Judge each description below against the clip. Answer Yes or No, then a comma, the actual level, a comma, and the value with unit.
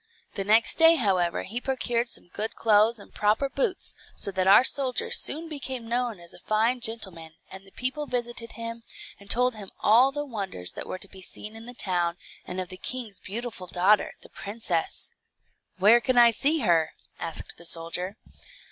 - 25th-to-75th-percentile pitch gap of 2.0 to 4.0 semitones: No, average, 4.7 semitones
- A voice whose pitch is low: No, high, 220 Hz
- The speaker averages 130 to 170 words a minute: No, average, 185 wpm